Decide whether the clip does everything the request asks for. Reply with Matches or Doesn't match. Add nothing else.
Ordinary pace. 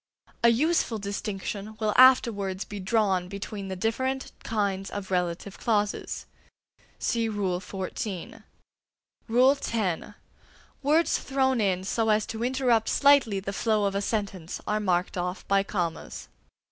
Doesn't match